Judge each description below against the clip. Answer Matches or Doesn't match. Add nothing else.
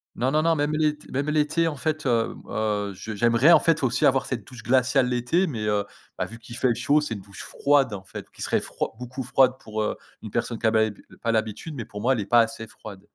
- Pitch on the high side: Doesn't match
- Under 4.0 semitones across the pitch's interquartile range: Doesn't match